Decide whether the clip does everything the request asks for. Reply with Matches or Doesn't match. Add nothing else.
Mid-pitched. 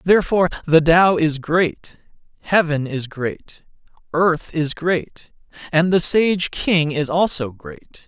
Matches